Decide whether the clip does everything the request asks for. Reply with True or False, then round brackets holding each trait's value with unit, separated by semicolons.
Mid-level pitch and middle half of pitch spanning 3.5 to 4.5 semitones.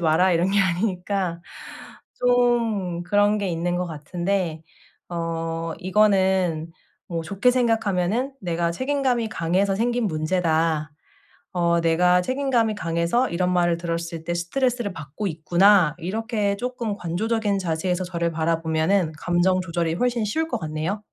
True (180 Hz; 4.0 semitones)